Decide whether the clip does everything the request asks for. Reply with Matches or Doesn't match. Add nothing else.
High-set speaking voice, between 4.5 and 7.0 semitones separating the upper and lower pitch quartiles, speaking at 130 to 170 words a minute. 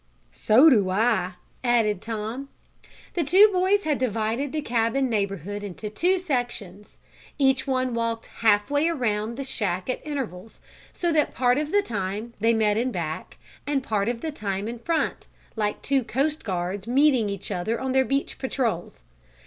Matches